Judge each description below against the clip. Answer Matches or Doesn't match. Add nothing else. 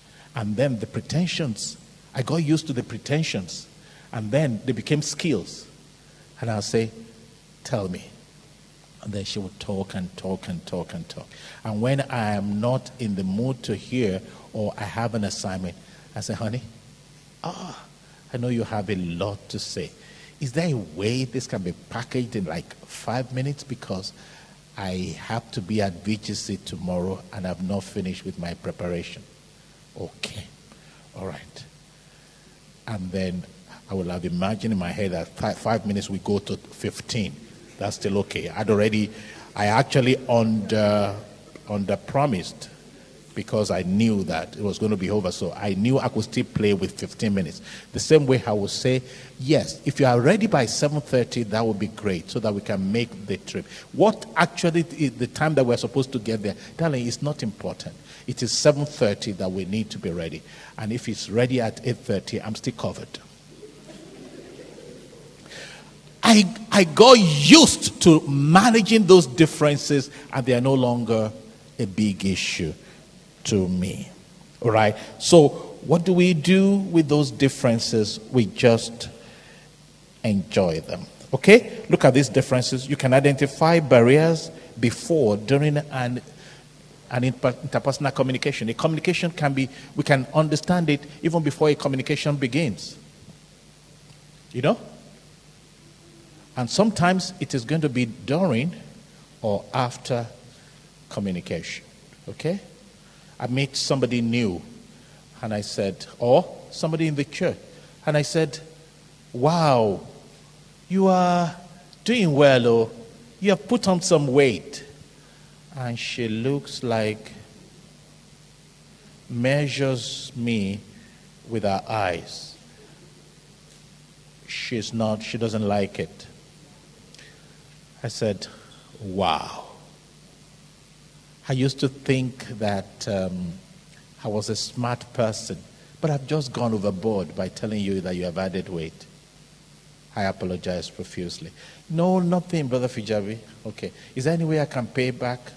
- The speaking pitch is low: Matches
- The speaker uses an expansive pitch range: Matches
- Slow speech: Doesn't match